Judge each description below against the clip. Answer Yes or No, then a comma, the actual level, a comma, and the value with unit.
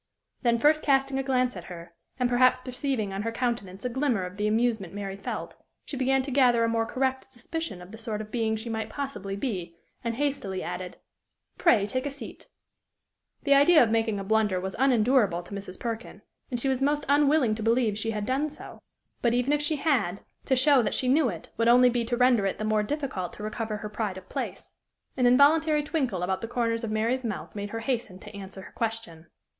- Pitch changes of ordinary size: Yes, average, 4.1 semitones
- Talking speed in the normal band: No, fast, 220 wpm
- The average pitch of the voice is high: Yes, high, 230 Hz